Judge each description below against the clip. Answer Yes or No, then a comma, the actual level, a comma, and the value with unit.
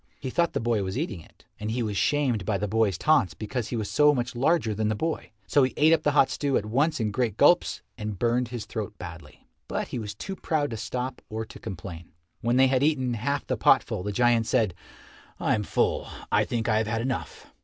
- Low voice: Yes, low, 120 Hz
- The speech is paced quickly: Yes, fast, 240 wpm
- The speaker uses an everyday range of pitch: Yes, average, 4.3 semitones